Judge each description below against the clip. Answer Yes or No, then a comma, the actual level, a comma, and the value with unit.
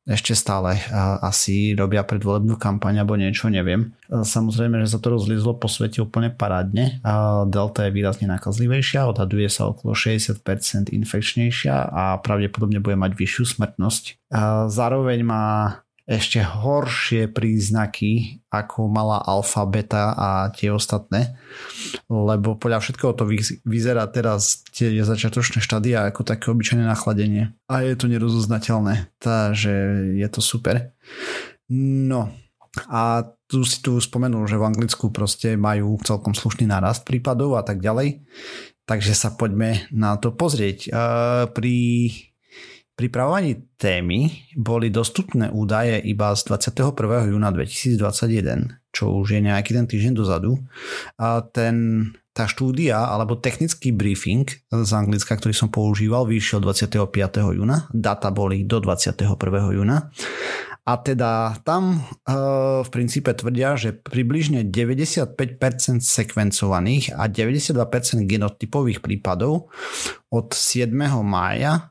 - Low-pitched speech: Yes, low, 115 Hz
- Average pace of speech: Yes, average, 120 wpm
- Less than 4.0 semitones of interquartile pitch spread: Yes, average, 2.8 semitones